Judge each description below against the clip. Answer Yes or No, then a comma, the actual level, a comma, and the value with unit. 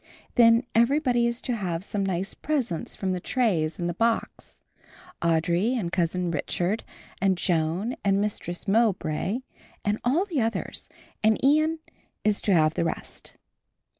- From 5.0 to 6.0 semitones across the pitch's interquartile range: Yes, average, 5.3 semitones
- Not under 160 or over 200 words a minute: No, average, 145 wpm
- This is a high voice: Yes, high, 200 Hz